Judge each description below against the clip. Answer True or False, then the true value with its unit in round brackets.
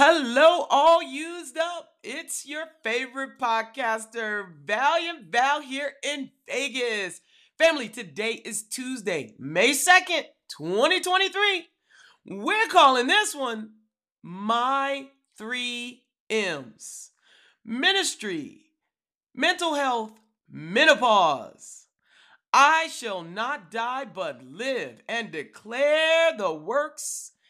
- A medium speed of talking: False (90 wpm)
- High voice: True (275 Hz)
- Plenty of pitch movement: True (5.8 semitones)